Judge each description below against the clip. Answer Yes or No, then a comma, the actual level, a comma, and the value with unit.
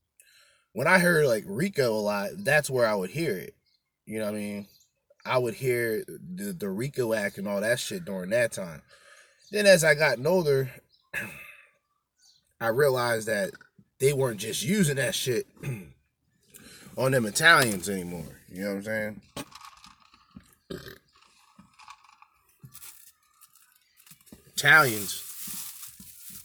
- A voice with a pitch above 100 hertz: Yes, medium, 140 Hz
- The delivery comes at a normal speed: No, slow, 125 wpm